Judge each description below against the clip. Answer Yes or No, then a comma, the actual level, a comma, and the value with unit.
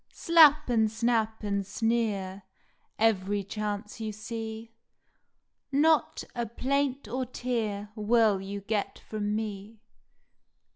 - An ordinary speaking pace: No, slow, 105 wpm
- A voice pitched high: Yes, high, 220 Hz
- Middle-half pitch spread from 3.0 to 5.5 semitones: No, narrow, 2.5 semitones